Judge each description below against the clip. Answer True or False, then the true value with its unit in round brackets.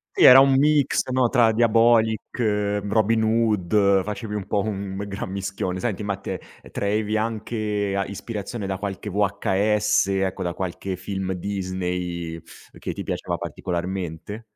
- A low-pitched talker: True (100 Hz)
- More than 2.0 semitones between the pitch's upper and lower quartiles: True (2.5 semitones)